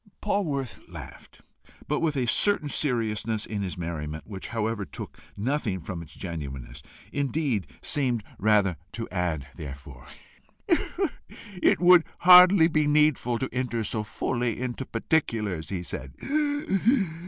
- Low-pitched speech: Yes, low, 115 Hz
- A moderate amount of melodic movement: No, wide, 8.3 semitones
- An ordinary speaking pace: No, slow, 125 wpm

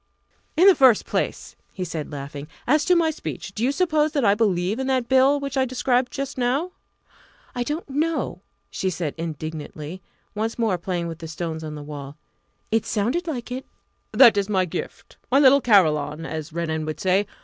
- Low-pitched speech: No, high, 210 Hz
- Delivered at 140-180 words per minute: No, average, 190 wpm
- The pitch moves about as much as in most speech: No, wide, 8.5 semitones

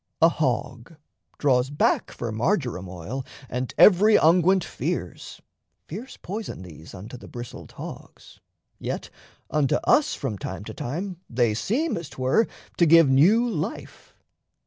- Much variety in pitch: Yes, wide, 7.3 semitones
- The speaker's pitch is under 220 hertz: Yes, medium, 140 Hz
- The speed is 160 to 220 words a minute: No, slow, 135 wpm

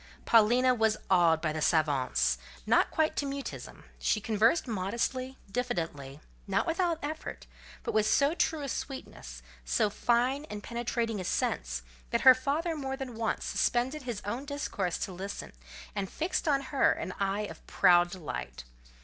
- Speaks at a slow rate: No, average, 160 wpm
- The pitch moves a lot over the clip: Yes, wide, 6.9 semitones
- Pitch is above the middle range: Yes, high, 225 Hz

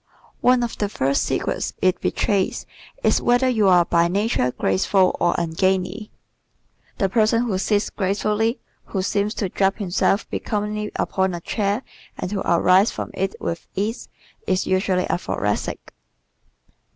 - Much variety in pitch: No, narrow, 2.5 semitones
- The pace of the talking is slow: No, average, 145 wpm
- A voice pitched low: No, high, 195 Hz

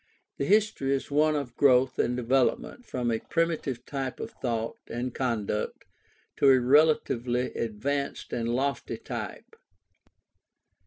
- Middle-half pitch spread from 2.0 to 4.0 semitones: Yes, average, 2.9 semitones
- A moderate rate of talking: No, slow, 125 wpm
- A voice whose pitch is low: Yes, low, 130 Hz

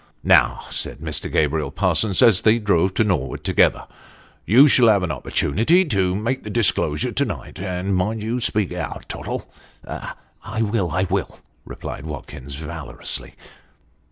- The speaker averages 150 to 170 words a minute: Yes, average, 155 wpm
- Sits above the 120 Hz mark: No, very low, 95 Hz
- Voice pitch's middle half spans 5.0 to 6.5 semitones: Yes, wide, 5.5 semitones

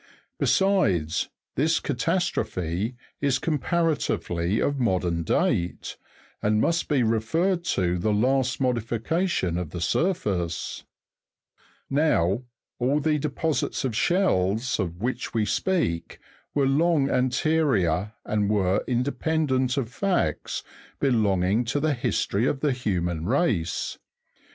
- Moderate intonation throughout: No, wide, 7.7 semitones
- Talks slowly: Yes, slow, 110 wpm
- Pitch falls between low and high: No, low, 125 Hz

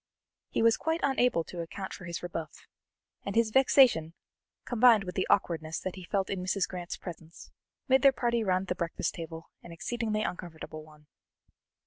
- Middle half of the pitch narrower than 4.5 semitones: No, wide, 5.5 semitones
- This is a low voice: No, medium, 185 Hz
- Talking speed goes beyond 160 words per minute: Yes, average, 170 wpm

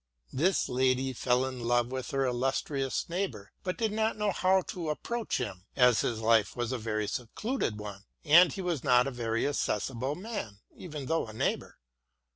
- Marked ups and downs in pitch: Yes, wide, 6.8 semitones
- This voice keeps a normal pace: Yes, average, 180 wpm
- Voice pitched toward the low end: Yes, low, 130 Hz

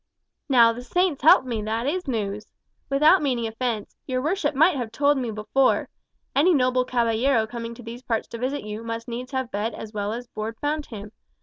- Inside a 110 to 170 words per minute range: No, average, 200 wpm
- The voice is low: No, high, 245 Hz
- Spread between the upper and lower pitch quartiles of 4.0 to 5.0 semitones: No, average, 3.5 semitones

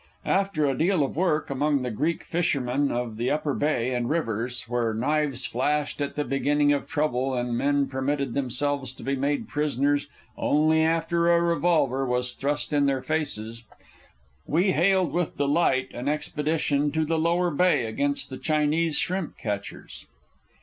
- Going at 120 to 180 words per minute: Yes, average, 160 wpm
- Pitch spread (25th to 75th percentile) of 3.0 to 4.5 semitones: Yes, average, 3.4 semitones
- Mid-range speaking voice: Yes, medium, 145 Hz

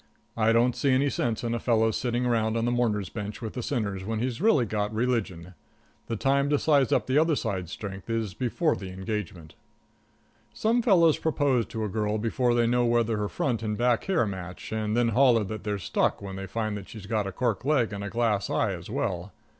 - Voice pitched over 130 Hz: No, low, 115 Hz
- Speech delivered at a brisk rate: Yes, fast, 225 wpm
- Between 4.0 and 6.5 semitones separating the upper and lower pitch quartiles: No, average, 3.1 semitones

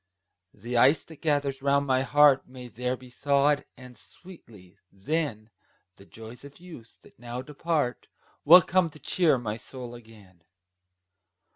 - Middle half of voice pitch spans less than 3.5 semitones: No, average, 3.9 semitones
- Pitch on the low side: Yes, low, 130 Hz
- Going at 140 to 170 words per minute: Yes, average, 145 wpm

